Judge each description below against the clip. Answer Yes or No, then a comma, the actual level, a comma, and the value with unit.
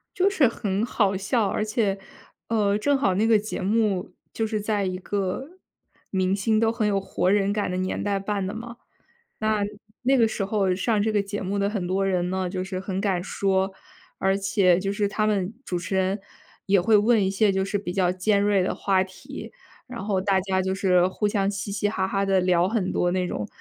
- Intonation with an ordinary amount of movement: No, narrow, 2.1 semitones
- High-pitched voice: Yes, high, 200 Hz